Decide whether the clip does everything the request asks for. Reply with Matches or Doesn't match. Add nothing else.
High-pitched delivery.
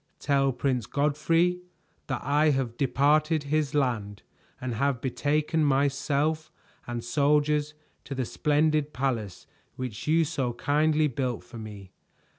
Doesn't match